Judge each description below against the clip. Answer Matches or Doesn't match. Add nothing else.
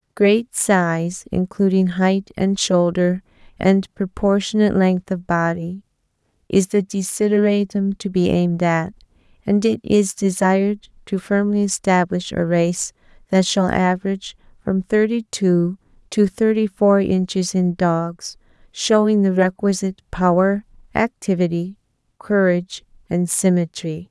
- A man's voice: Doesn't match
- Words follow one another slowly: Matches